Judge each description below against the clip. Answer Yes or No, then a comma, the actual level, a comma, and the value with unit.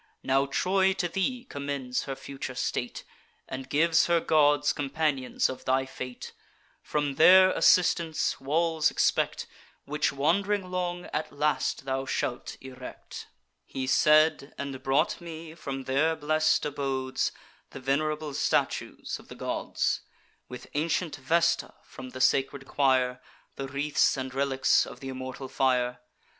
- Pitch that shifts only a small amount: No, average, 3.3 semitones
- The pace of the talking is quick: No, slow, 135 wpm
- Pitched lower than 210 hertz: Yes, medium, 140 Hz